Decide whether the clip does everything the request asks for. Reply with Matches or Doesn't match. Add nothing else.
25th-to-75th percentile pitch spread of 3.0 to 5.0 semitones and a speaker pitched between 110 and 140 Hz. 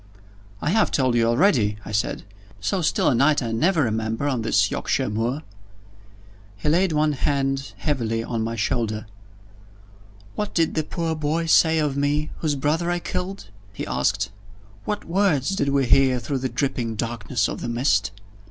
Doesn't match